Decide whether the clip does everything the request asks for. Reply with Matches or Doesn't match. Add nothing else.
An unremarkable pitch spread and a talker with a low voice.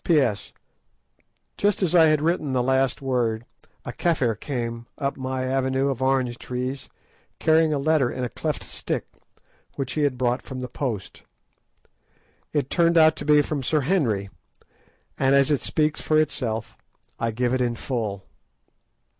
Matches